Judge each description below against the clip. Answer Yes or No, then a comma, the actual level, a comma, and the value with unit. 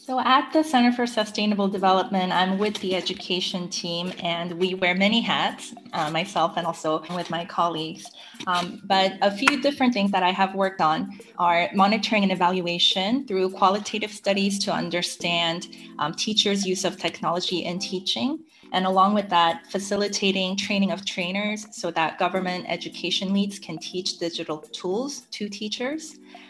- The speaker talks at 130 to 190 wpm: Yes, average, 160 wpm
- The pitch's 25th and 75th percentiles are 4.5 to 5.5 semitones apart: No, average, 3.2 semitones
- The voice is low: No, high, 190 Hz